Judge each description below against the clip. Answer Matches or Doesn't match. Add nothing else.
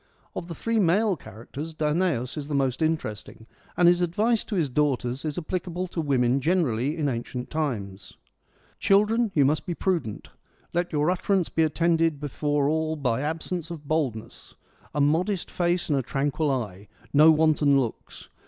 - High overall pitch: Doesn't match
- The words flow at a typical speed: Matches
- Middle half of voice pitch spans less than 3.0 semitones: Doesn't match